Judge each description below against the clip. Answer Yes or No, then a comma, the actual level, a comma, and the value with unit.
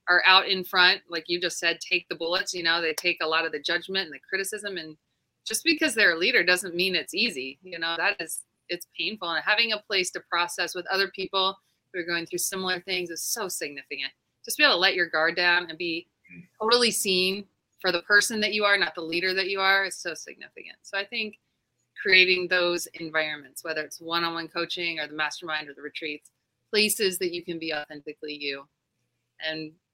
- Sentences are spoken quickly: Yes, fast, 215 wpm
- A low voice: No, medium, 175 Hz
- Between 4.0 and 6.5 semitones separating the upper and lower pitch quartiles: No, average, 3.2 semitones